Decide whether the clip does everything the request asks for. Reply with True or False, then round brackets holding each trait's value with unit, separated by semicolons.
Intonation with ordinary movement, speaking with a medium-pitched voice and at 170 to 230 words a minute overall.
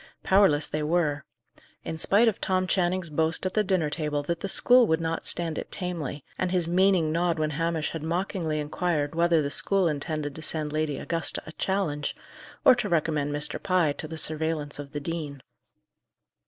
True (3.1 semitones; 160 Hz; 185 wpm)